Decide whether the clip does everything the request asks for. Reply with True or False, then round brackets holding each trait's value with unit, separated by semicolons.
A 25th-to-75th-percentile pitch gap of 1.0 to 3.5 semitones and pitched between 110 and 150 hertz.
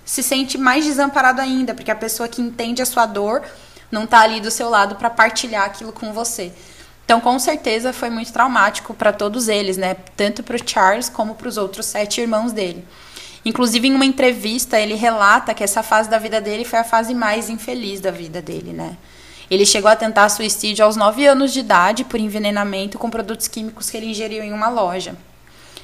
False (2.4 semitones; 225 Hz)